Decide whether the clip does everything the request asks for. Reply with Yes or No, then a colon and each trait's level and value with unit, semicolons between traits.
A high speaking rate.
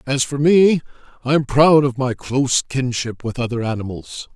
No: average, 180 wpm